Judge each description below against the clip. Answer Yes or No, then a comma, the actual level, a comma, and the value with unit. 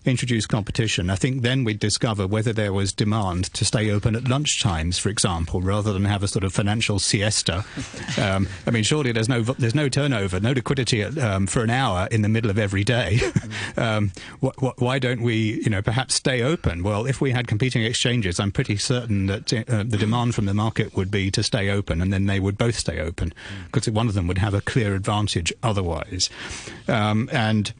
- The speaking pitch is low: Yes, low, 110 Hz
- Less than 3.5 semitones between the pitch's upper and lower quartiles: No, average, 3.8 semitones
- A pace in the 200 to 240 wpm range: Yes, fast, 205 wpm